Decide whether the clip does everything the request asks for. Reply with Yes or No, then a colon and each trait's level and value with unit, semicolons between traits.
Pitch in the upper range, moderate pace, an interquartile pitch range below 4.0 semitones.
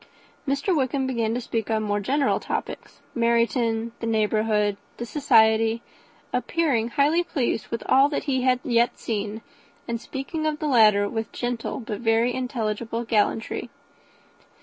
Yes: high, 235 Hz; average, 150 wpm; average, 2.9 semitones